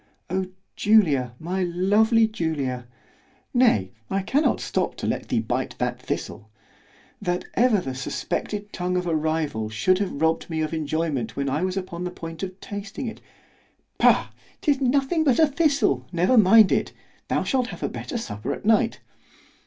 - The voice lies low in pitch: No, medium, 180 Hz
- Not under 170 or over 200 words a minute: No, average, 155 wpm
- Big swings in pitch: Yes, wide, 6.2 semitones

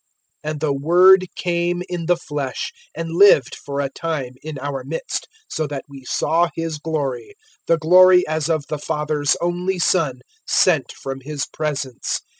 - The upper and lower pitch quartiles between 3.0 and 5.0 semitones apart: Yes, average, 3.4 semitones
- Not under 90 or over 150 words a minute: No, average, 165 wpm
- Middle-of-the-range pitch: Yes, medium, 155 Hz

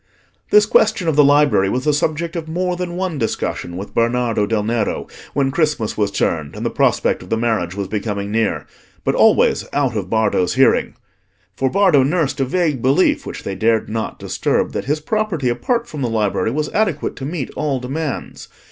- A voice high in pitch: No, low, 135 Hz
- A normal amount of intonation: No, wide, 6.3 semitones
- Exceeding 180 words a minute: Yes, average, 190 wpm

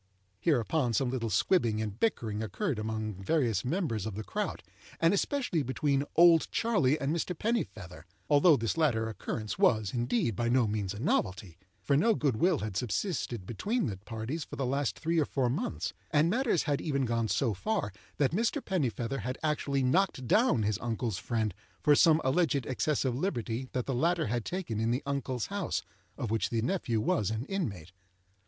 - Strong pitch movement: Yes, wide, 6.5 semitones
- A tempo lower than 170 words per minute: No, average, 185 wpm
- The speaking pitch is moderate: No, low, 130 Hz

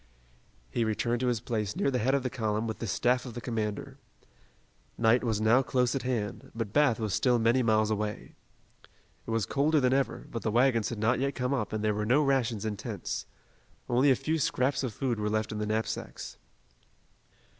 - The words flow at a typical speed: No, fast, 210 wpm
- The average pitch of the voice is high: No, low, 115 Hz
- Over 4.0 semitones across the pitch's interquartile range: No, average, 3.0 semitones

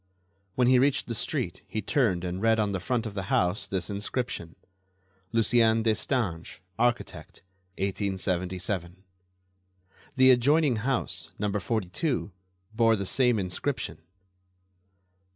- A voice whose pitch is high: No, low, 105 Hz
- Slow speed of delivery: Yes, slow, 115 wpm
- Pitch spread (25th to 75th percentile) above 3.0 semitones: Yes, average, 4.7 semitones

